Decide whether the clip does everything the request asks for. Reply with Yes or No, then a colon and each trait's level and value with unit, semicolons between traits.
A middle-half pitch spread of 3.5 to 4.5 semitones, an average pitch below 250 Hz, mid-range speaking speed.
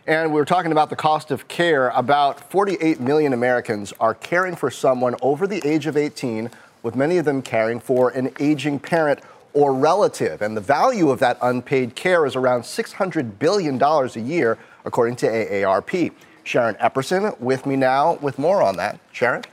Yes: average, 4.0 semitones; medium, 140 Hz; average, 180 wpm